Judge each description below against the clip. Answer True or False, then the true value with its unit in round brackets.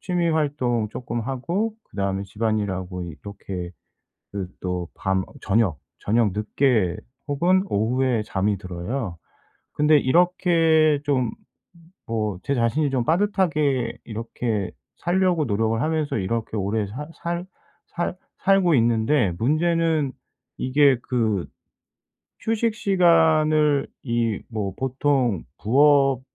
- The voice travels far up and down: True (6.7 semitones)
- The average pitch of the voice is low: True (125 Hz)